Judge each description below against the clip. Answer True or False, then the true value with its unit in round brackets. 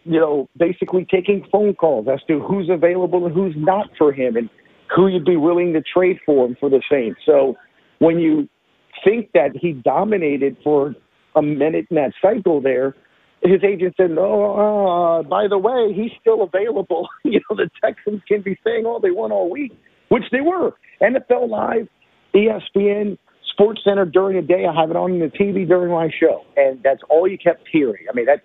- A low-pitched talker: False (185 Hz)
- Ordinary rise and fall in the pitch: True (4.3 semitones)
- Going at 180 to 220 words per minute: True (195 wpm)